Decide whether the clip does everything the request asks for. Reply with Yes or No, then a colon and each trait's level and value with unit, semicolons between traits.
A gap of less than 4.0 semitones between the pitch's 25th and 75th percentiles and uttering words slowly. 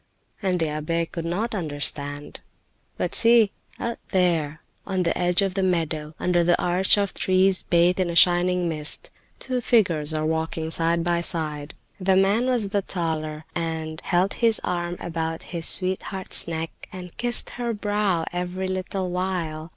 No: average, 2.8 semitones; average, 160 wpm